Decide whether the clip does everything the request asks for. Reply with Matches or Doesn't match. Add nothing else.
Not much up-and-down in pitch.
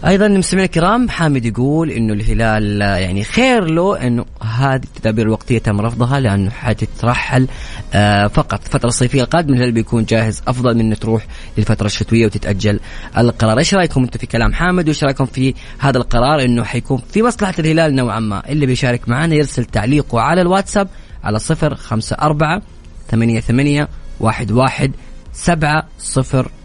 Doesn't match